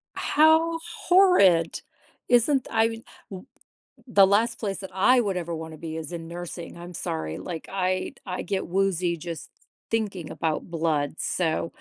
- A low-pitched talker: No, medium, 185 Hz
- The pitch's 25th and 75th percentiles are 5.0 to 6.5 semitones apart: Yes, average, 5.3 semitones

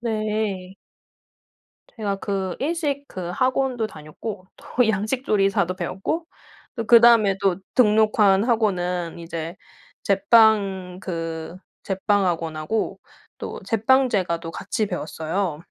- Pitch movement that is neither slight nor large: Yes, average, 3.8 semitones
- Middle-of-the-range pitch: No, high, 200 Hz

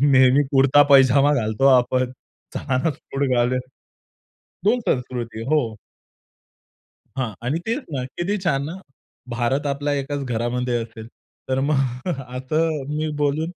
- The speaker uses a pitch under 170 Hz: Yes, low, 135 Hz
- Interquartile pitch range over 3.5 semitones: No, average, 2.8 semitones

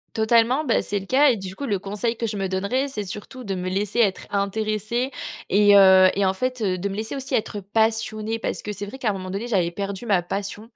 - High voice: Yes, high, 210 Hz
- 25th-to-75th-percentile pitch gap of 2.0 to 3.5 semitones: Yes, average, 2.8 semitones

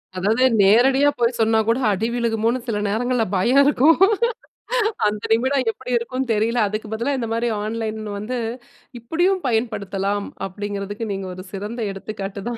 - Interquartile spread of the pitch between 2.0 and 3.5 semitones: Yes, average, 3.1 semitones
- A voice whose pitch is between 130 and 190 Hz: No, high, 225 Hz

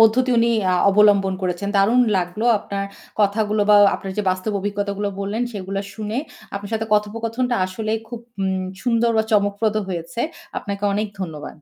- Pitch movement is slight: Yes, narrow, 2.2 semitones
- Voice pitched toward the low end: No, high, 205 Hz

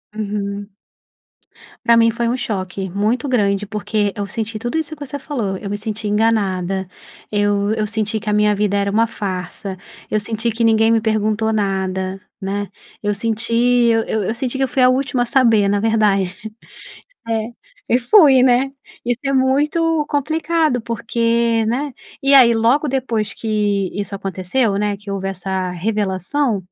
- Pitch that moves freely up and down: No, average, 3.2 semitones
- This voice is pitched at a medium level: No, high, 220 Hz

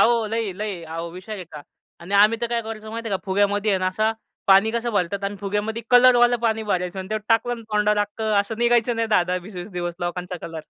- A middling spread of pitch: Yes, average, 3.4 semitones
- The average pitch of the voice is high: Yes, high, 210 Hz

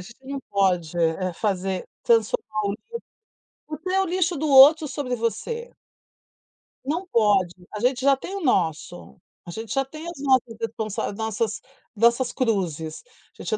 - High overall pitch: Yes, high, 230 Hz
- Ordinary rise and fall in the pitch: No, wide, 6.9 semitones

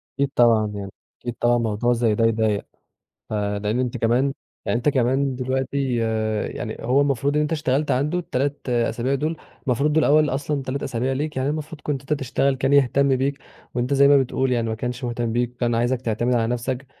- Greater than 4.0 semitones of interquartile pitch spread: No, average, 2.8 semitones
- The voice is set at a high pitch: No, low, 130 Hz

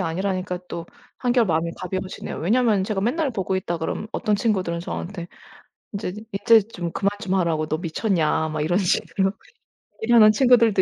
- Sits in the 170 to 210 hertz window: Yes, high, 190 Hz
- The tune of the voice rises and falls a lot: No, average, 4.1 semitones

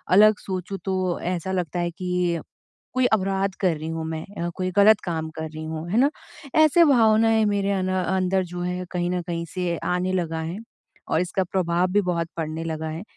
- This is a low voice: No, medium, 180 Hz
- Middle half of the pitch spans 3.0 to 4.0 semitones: No, narrow, 2.5 semitones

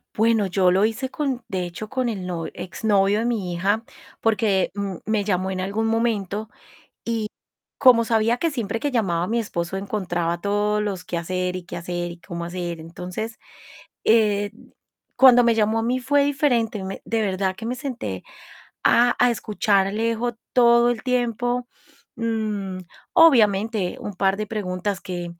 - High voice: Yes, high, 210 Hz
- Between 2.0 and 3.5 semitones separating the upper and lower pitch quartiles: No, average, 3.9 semitones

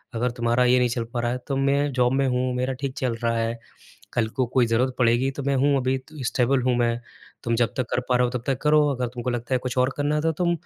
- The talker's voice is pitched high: No, low, 125 Hz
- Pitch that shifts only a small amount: Yes, narrow, 2.1 semitones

